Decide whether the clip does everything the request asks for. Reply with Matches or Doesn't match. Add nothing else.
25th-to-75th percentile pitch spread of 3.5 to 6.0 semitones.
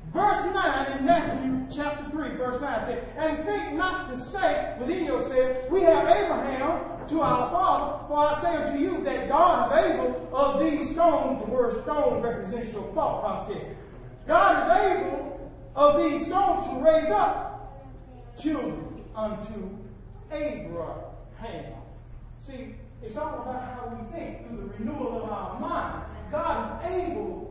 Matches